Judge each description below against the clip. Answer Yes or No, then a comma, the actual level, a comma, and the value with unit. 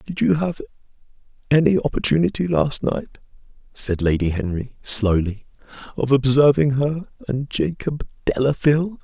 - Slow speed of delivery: Yes, slow, 115 wpm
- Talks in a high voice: No, low, 135 Hz